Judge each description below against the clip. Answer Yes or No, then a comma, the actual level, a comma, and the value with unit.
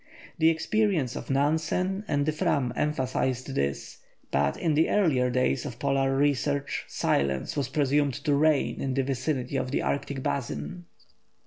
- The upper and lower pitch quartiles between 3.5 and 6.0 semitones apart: No, average, 2.9 semitones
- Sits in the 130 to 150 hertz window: Yes, medium, 140 Hz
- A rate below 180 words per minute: Yes, average, 150 wpm